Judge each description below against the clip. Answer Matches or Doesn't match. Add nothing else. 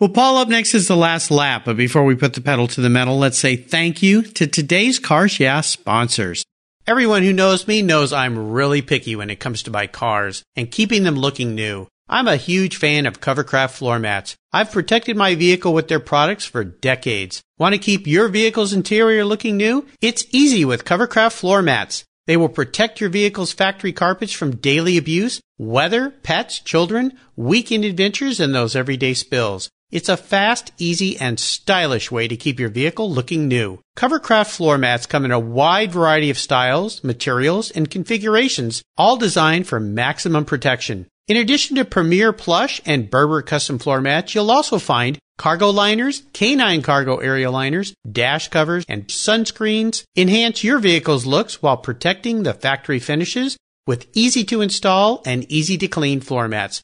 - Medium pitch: Matches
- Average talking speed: Matches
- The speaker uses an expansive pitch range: Matches